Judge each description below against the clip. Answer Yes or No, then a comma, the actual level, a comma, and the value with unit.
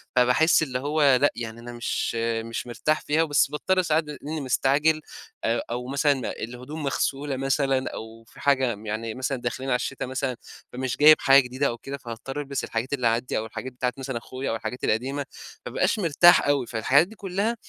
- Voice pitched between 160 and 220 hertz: No, low, 135 Hz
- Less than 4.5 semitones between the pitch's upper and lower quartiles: Yes, average, 3.2 semitones